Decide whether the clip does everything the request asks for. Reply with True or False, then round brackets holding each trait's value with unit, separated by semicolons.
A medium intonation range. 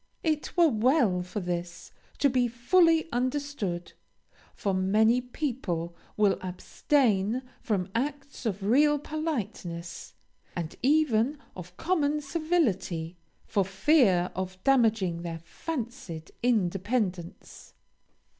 False (7.7 semitones)